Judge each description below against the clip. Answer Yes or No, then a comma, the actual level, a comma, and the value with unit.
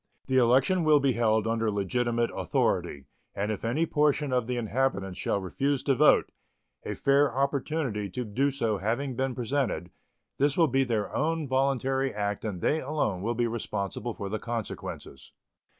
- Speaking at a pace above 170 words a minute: No, average, 165 wpm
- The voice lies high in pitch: No, low, 125 Hz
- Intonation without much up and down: No, average, 4.2 semitones